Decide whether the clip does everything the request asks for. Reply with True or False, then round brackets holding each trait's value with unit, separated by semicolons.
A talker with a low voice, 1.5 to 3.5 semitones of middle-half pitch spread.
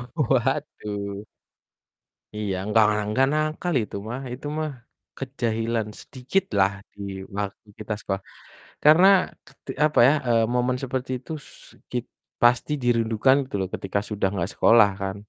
False (115 Hz; 4.3 semitones)